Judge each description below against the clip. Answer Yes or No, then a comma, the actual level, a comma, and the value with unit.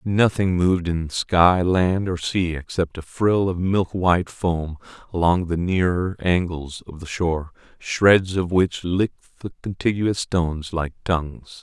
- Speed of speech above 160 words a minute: No, average, 150 wpm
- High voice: No, very low, 90 Hz